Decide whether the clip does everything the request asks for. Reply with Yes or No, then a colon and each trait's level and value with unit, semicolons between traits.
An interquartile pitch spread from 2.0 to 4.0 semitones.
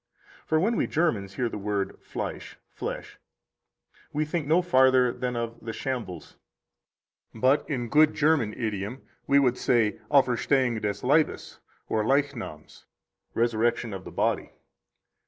No: average, 4.5 semitones